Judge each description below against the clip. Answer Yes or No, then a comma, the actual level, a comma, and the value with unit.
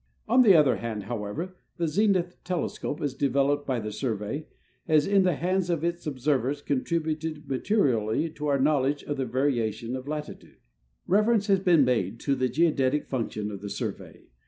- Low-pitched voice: No, medium, 145 Hz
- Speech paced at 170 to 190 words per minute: Yes, average, 180 wpm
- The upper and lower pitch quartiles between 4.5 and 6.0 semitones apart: Yes, average, 4.9 semitones